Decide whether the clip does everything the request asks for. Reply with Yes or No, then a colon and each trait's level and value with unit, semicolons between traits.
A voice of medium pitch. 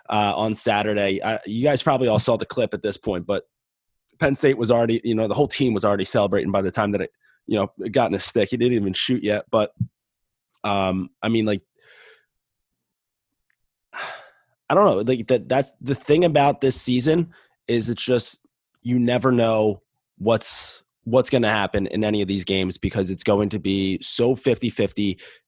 No: low, 110 Hz